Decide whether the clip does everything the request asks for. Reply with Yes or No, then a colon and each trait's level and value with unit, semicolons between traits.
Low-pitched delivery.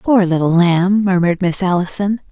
No: medium, 185 Hz